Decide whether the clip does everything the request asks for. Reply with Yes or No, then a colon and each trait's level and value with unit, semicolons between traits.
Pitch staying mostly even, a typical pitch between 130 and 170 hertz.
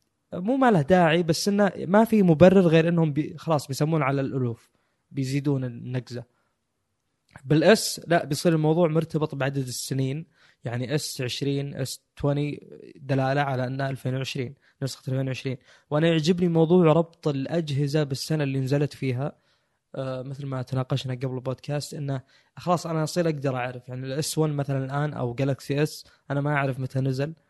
No: average, 3.3 semitones; medium, 140 Hz